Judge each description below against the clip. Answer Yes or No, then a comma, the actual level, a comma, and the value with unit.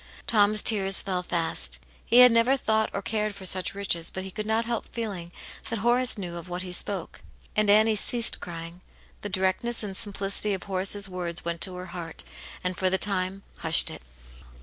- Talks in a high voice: Yes, high, 195 Hz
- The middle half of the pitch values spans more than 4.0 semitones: No, average, 2.9 semitones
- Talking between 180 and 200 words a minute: Yes, average, 195 wpm